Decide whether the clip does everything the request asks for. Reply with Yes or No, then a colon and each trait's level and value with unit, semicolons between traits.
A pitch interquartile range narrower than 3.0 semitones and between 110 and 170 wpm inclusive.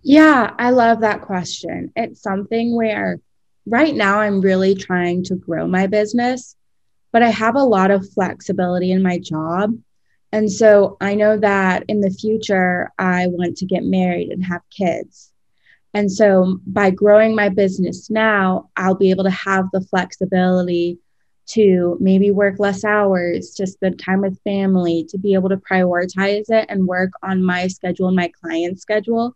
Yes: narrow, 2.4 semitones; average, 165 wpm